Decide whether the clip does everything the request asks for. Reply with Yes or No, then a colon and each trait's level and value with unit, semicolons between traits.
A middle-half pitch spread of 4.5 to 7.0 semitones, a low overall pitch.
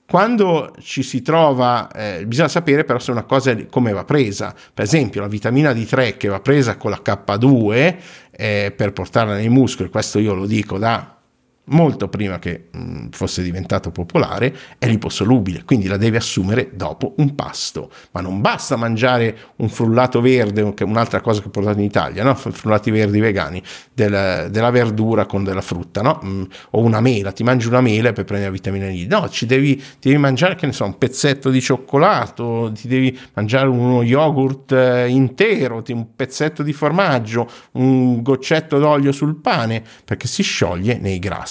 Yes: average, 4.8 semitones; low, 120 Hz